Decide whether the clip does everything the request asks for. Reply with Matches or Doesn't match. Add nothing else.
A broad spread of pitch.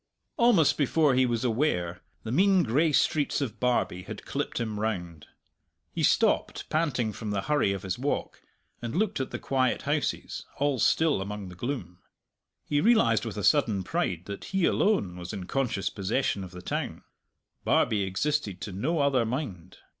Matches